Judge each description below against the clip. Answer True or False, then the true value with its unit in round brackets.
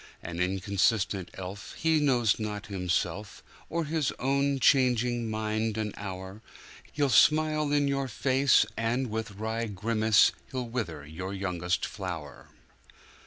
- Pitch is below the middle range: True (110 Hz)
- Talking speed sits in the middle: False (115 wpm)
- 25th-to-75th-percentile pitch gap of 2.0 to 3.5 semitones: False (5.3 semitones)